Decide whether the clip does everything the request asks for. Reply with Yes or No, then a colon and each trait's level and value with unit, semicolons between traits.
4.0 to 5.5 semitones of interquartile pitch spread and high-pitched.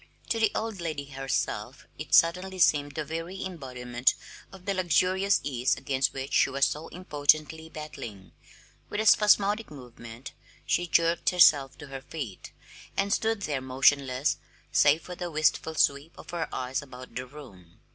No: average, 5.1 semitones; medium, 150 Hz